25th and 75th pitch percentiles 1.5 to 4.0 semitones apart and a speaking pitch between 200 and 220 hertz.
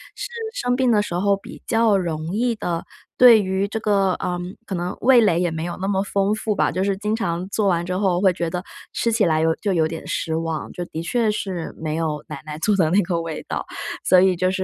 No: average, 3.7 semitones; medium, 185 Hz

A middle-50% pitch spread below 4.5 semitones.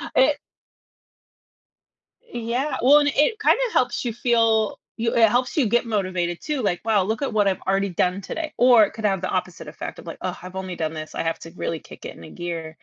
No: average, 5.1 semitones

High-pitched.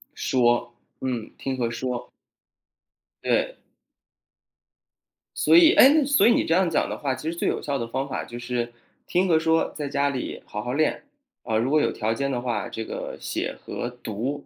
No: low, 130 Hz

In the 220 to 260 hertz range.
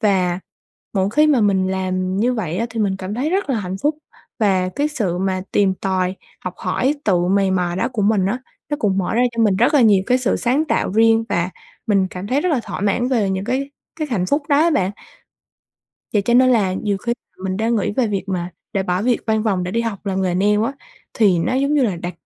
No: high, 205 Hz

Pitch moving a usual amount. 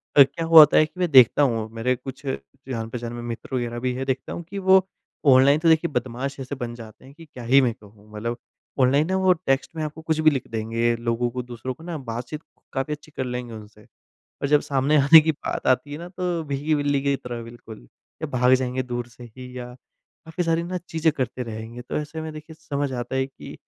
Yes: average, 4.1 semitones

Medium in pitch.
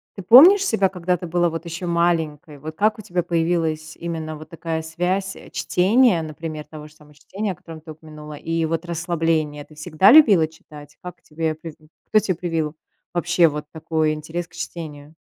Yes: medium, 165 Hz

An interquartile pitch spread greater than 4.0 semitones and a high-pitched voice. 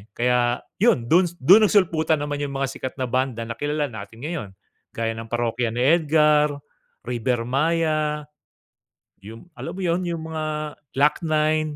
No: average, 4.5 semitones; medium, 150 Hz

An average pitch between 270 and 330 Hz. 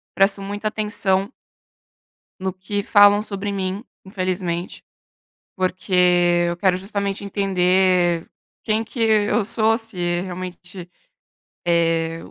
No: high, 190 Hz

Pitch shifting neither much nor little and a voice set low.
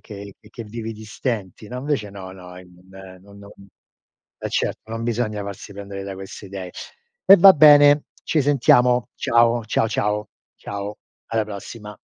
Yes: average, 3.2 semitones; low, 105 Hz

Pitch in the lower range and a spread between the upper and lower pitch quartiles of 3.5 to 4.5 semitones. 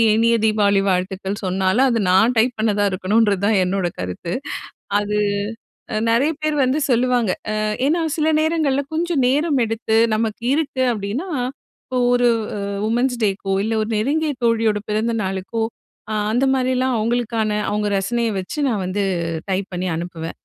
No: high, 220 Hz; average, 4.2 semitones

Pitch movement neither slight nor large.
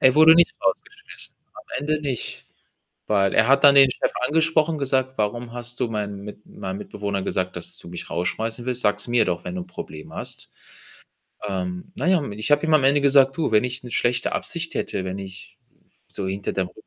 No: wide, 6.3 semitones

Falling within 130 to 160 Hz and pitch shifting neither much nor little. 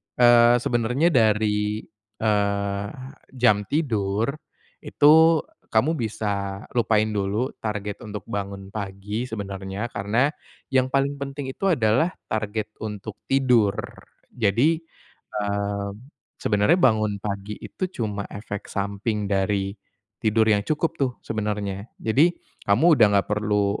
No: low, 105 Hz; average, 3.4 semitones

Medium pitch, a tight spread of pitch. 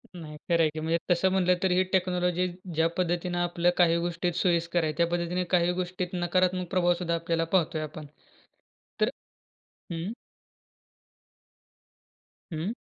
Yes: medium, 175 Hz; narrow, 1.4 semitones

